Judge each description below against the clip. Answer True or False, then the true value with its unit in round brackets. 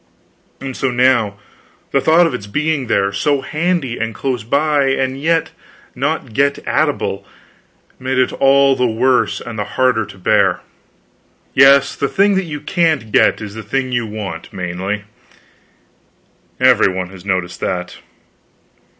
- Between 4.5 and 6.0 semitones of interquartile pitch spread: True (5.1 semitones)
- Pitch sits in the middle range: False (130 Hz)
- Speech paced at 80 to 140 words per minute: False (155 wpm)